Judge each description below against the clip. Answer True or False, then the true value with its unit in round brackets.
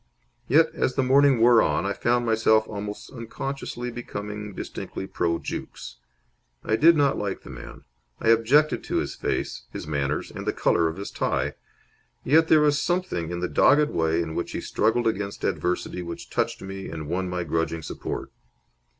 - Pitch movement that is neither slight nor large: False (6.5 semitones)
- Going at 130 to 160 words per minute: False (175 wpm)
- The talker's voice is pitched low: True (110 Hz)